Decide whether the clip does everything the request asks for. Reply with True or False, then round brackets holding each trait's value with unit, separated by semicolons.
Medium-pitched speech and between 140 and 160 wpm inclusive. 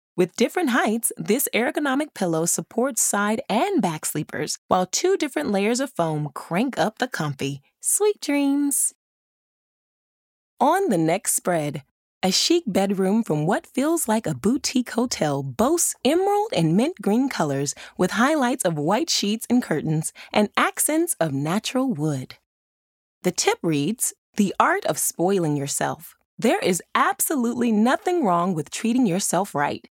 False (210 Hz; 145 wpm)